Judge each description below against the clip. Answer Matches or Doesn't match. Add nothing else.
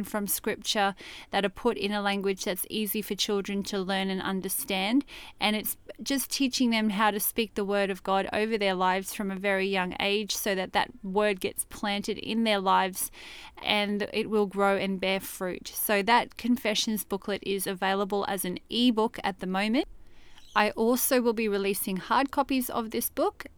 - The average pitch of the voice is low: Doesn't match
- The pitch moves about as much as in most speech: Doesn't match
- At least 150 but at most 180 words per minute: Doesn't match